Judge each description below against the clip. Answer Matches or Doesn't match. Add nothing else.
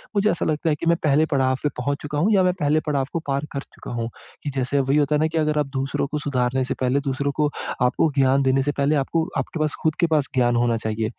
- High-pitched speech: Doesn't match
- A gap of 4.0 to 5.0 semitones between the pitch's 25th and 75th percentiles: Doesn't match